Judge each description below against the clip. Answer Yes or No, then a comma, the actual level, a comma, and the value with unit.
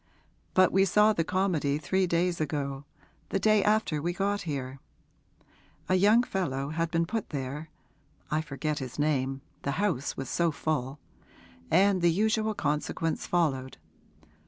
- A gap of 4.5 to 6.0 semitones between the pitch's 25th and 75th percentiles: Yes, average, 5.2 semitones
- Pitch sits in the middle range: Yes, medium, 165 Hz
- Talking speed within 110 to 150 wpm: Yes, average, 145 wpm